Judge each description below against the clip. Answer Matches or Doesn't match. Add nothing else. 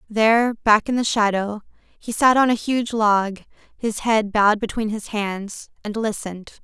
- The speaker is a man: Doesn't match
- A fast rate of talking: Doesn't match